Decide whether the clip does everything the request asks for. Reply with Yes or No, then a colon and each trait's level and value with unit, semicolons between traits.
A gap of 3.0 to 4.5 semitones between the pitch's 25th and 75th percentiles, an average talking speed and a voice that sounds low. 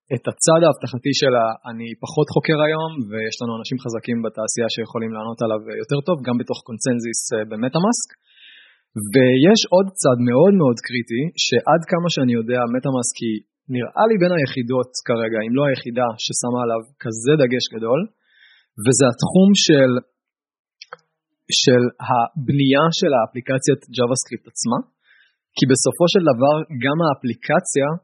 Yes: average, 4.2 semitones; average, 135 wpm; low, 130 Hz